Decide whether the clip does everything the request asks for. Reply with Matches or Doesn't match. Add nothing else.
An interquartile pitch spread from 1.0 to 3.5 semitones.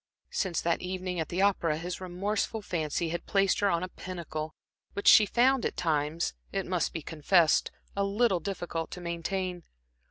Matches